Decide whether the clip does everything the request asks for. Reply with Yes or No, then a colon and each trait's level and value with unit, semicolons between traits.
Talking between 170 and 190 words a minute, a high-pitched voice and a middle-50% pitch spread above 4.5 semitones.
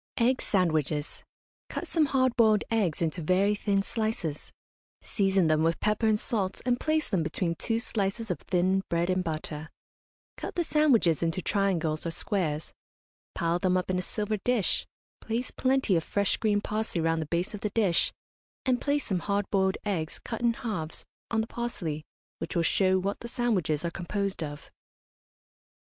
Yes: average, 175 wpm; high, 195 Hz; average, 5.0 semitones